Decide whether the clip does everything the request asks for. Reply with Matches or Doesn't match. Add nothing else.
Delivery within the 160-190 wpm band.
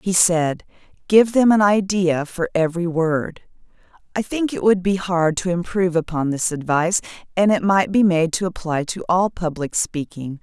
Matches